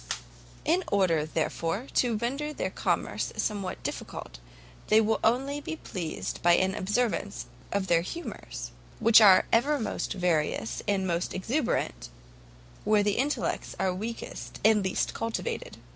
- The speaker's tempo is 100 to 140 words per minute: Yes, slow, 135 wpm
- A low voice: No, high, 205 Hz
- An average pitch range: Yes, average, 4.8 semitones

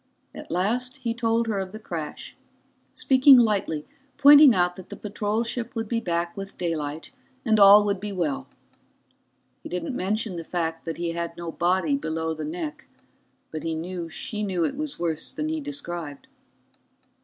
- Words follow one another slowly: No, average, 175 wpm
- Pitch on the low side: No, medium, 185 Hz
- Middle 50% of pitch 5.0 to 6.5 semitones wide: Yes, average, 5.3 semitones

